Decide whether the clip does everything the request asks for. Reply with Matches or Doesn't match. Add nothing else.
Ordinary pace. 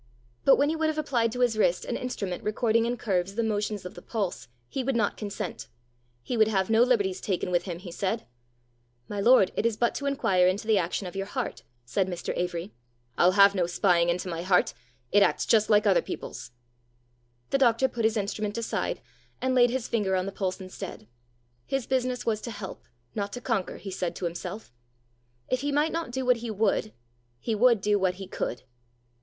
Doesn't match